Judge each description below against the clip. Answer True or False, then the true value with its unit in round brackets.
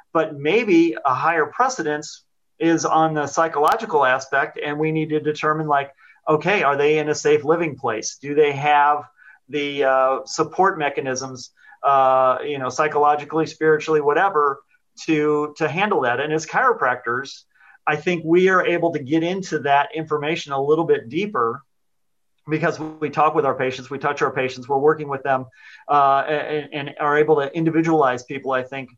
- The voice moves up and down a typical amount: False (2.1 semitones)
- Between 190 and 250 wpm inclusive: False (170 wpm)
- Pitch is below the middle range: False (150 Hz)